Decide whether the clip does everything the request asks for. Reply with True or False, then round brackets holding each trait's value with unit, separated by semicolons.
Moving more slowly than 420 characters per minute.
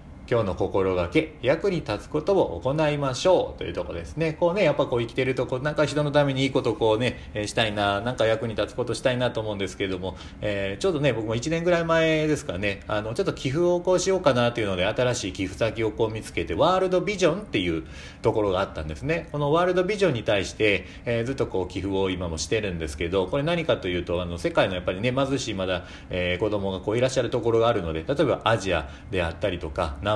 False (500 characters per minute)